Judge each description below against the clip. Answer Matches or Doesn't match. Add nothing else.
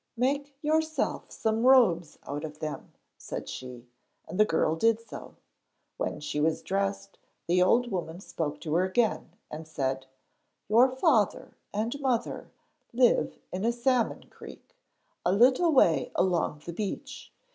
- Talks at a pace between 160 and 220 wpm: Doesn't match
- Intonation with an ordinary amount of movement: Doesn't match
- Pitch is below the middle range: Doesn't match